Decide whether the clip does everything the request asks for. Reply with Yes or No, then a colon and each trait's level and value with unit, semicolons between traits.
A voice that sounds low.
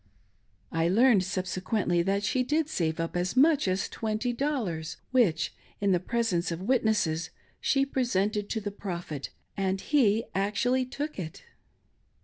No: high, 200 Hz